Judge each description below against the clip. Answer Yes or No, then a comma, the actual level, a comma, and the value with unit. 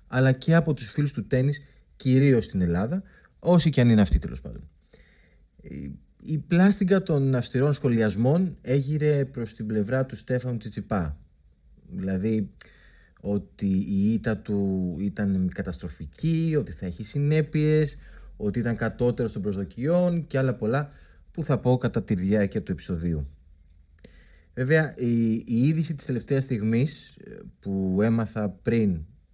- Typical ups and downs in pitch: No, wide, 6.3 semitones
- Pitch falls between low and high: No, low, 115 Hz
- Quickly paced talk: No, average, 135 wpm